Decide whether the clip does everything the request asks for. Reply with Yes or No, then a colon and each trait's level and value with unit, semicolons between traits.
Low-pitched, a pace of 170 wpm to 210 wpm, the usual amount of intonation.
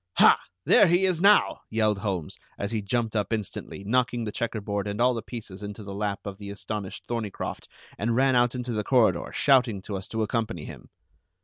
Yes: low, 110 Hz; average, 200 wpm; average, 3.2 semitones